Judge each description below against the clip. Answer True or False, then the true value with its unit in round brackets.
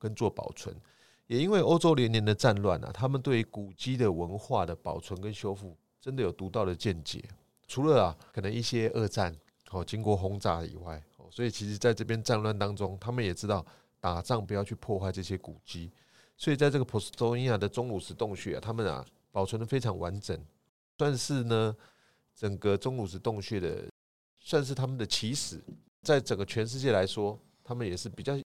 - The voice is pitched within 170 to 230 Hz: False (105 Hz)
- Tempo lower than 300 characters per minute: False (305 characters per minute)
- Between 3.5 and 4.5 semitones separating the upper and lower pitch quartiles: True (4.2 semitones)